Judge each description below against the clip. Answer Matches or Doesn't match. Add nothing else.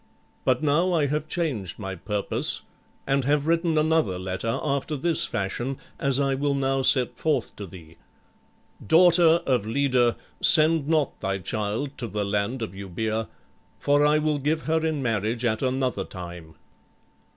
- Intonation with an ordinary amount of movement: Doesn't match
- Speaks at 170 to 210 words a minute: Doesn't match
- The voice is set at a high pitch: Doesn't match